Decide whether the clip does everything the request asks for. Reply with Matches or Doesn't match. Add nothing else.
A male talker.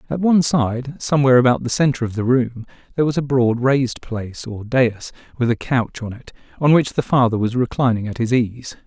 Matches